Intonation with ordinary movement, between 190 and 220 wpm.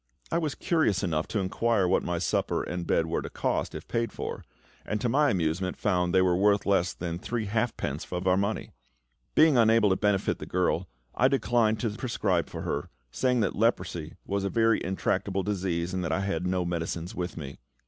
Yes: average, 4.1 semitones; average, 200 wpm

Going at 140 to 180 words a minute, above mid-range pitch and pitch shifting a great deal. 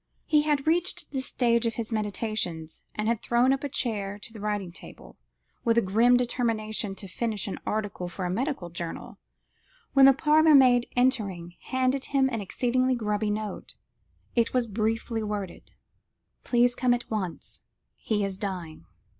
No: average, 160 wpm; high, 225 Hz; average, 3.8 semitones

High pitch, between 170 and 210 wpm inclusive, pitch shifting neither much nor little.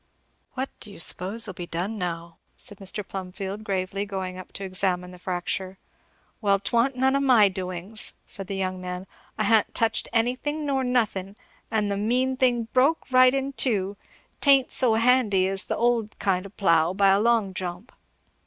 Yes: high, 200 Hz; average, 175 wpm; average, 4.5 semitones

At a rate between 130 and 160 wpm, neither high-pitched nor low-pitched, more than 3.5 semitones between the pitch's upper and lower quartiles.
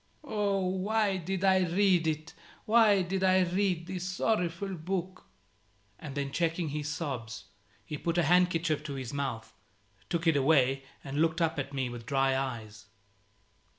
Yes: average, 155 wpm; medium, 165 Hz; average, 5.0 semitones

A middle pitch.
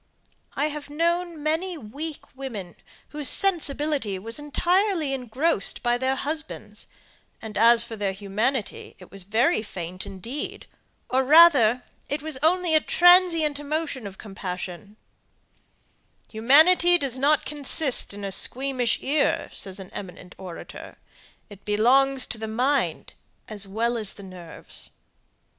No: very high, 260 Hz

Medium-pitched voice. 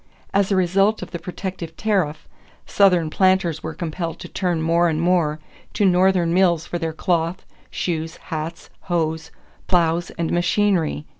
Yes: medium, 175 Hz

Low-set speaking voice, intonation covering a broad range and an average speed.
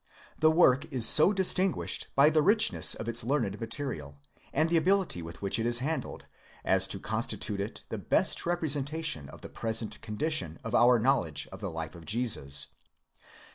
Yes: low, 125 Hz; wide, 7.5 semitones; average, 175 wpm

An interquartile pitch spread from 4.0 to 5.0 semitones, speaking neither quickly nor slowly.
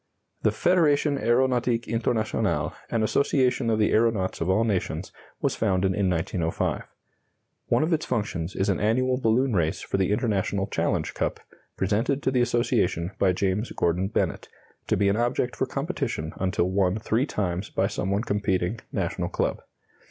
Yes: average, 4.4 semitones; average, 160 wpm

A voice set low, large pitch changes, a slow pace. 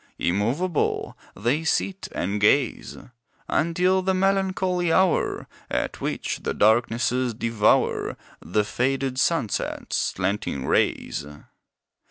Yes: low, 130 Hz; wide, 8.8 semitones; slow, 95 wpm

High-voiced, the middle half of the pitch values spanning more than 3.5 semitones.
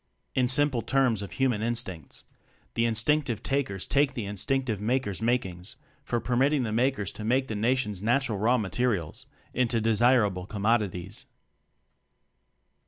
No: low, 115 Hz; average, 3.9 semitones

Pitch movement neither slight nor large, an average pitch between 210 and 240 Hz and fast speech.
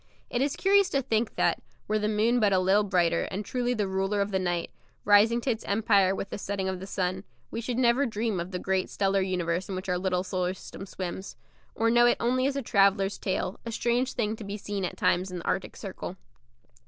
No: average, 3.6 semitones; high, 200 Hz; fast, 235 wpm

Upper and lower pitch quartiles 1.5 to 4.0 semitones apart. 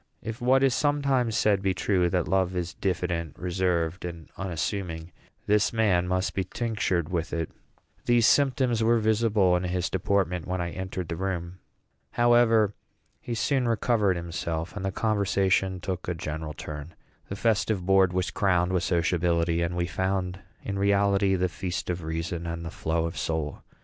Yes: average, 3.2 semitones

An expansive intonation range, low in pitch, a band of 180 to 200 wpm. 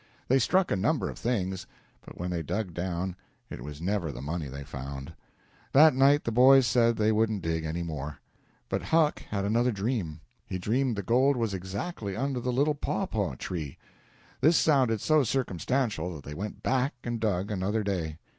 Yes: wide, 6.6 semitones; low, 105 Hz; average, 185 wpm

